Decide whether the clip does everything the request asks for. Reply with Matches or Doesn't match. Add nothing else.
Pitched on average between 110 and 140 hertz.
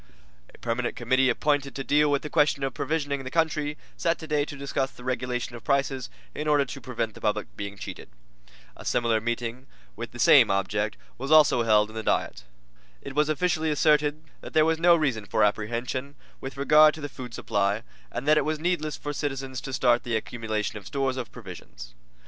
Matches